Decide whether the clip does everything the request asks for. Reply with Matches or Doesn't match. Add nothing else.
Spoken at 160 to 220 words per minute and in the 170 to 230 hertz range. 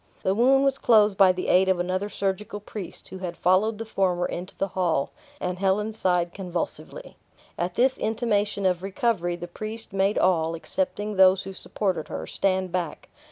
Matches